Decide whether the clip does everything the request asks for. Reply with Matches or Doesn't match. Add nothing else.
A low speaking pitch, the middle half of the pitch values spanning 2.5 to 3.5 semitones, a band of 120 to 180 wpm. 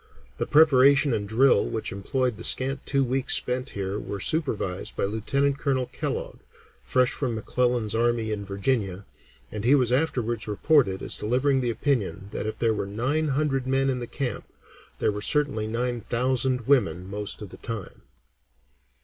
Doesn't match